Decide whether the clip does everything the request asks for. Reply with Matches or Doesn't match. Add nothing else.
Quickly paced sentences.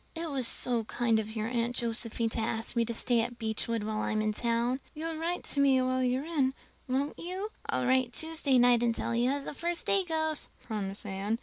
Matches